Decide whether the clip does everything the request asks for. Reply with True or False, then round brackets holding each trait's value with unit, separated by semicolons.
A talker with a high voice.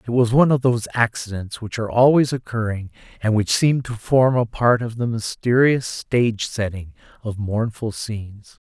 False (115 Hz)